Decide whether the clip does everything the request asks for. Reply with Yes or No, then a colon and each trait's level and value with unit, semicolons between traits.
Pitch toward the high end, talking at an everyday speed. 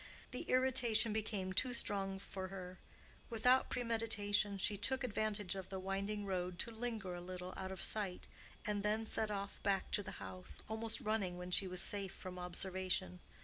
Yes: high, 200 Hz; average, 175 wpm